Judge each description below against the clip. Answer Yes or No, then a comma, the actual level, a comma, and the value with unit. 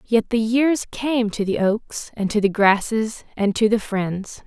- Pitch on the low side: No, high, 220 Hz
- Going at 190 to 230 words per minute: Yes, average, 200 wpm